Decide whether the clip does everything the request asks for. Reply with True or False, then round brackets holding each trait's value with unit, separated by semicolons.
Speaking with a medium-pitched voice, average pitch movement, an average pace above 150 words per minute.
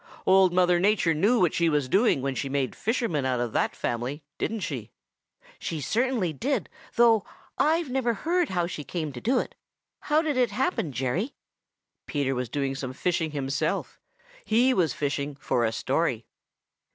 False (170 Hz; 9.0 semitones; 170 wpm)